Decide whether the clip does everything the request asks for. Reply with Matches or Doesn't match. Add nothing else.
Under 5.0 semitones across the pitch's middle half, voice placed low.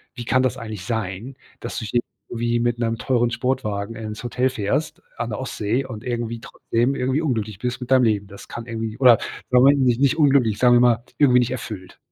Matches